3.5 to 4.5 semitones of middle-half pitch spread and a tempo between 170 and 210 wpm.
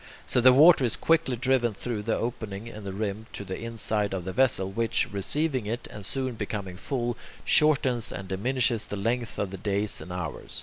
Yes: average, 3.9 semitones; average, 200 wpm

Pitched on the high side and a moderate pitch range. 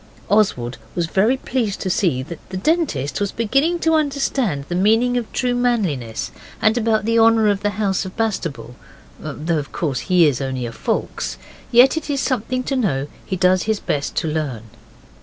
No: high, 205 Hz; wide, 7.9 semitones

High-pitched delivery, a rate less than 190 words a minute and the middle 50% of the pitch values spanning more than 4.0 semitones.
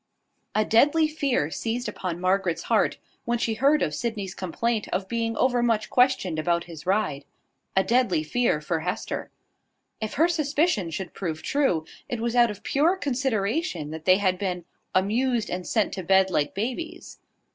Yes: high, 215 Hz; average, 165 wpm; wide, 5.5 semitones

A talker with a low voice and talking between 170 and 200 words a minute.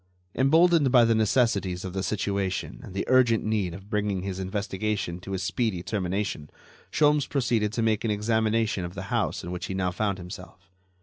Yes: low, 105 Hz; average, 185 wpm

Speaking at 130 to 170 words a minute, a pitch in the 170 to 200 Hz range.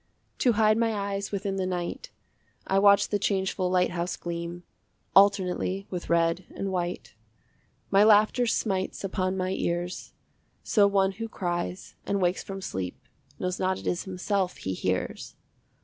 Yes: average, 150 wpm; high, 190 Hz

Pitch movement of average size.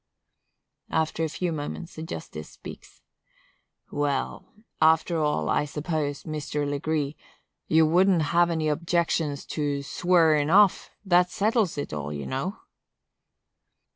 Yes: average, 3.0 semitones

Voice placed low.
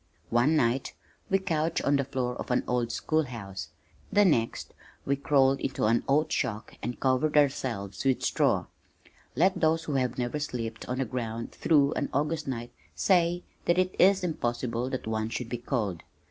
Yes: low, 130 Hz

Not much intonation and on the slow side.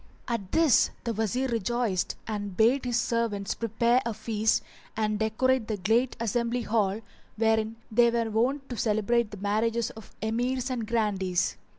No: narrow, 2.0 semitones; average, 155 wpm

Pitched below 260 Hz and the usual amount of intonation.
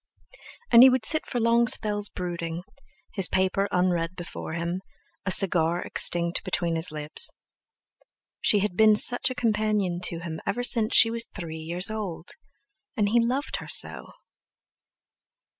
Yes: high, 190 Hz; average, 4.4 semitones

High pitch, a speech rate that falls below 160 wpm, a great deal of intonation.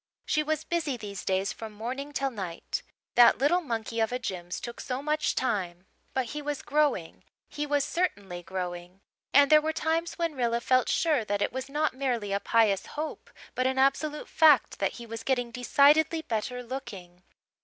No: very high, 255 Hz; average, 185 wpm; wide, 6.1 semitones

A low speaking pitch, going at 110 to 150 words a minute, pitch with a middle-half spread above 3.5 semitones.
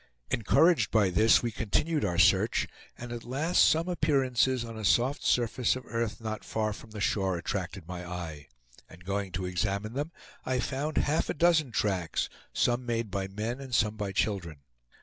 No: low, 110 Hz; average, 180 wpm; average, 4.9 semitones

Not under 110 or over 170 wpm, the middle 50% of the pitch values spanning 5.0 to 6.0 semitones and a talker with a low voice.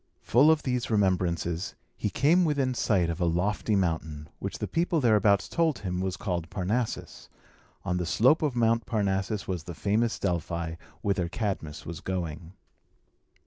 Yes: average, 155 wpm; average, 5.3 semitones; very low, 95 Hz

